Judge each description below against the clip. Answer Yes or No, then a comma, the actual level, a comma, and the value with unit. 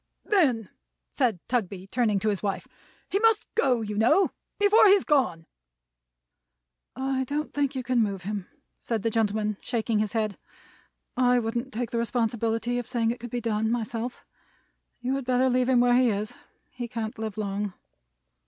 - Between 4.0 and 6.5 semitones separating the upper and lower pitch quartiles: No, average, 2.9 semitones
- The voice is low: No, high, 235 Hz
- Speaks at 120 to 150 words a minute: No, average, 170 wpm